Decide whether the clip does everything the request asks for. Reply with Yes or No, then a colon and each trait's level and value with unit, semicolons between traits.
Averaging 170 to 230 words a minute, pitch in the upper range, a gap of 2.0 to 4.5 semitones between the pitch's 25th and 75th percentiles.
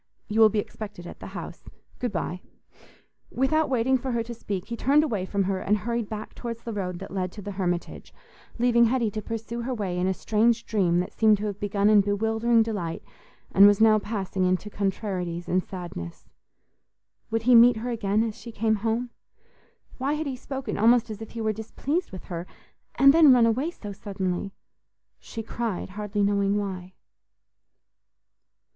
Yes: average, 185 wpm; high, 215 Hz; average, 3.2 semitones